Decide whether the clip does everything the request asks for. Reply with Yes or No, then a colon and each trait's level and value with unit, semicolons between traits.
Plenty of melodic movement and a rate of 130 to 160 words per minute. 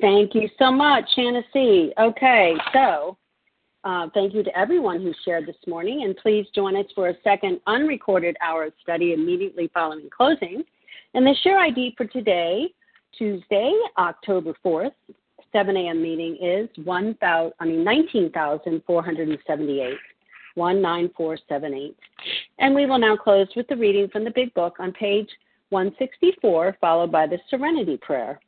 Yes: wide, 7.2 semitones; average, 145 wpm